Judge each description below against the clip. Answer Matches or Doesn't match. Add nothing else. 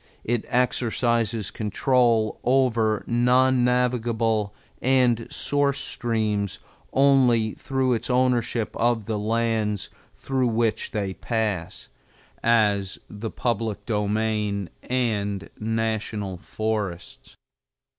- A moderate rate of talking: Doesn't match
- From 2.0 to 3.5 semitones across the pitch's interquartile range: Matches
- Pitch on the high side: Doesn't match